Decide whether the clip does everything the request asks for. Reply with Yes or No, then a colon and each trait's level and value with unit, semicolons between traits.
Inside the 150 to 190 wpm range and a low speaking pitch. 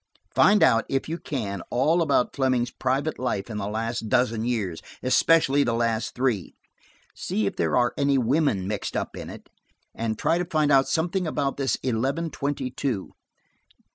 Yes: average, 170 wpm; low, 130 Hz